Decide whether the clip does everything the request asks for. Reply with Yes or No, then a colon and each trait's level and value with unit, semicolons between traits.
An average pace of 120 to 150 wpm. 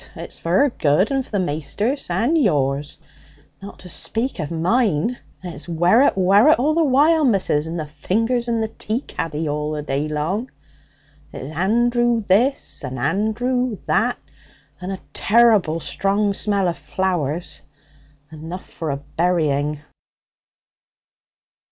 Yes: slow, 135 wpm